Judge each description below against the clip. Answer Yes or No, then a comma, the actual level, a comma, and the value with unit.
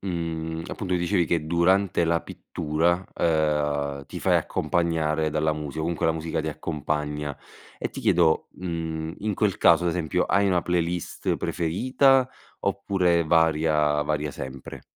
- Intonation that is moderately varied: No, narrow, 2.3 semitones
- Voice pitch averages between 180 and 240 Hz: No, very low, 80 Hz